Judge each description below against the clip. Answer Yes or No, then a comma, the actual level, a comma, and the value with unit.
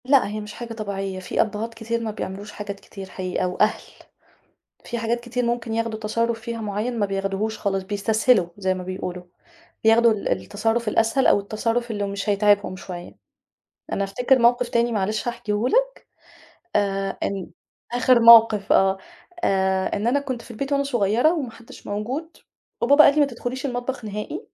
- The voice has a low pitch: No, high, 220 Hz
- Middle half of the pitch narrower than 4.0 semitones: Yes, average, 3.2 semitones